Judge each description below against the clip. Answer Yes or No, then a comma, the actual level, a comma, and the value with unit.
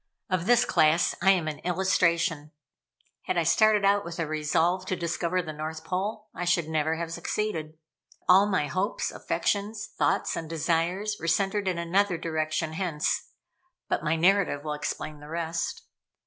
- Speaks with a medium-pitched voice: Yes, medium, 170 Hz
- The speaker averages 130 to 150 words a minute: No, average, 165 wpm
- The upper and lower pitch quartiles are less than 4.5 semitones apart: Yes, average, 3.3 semitones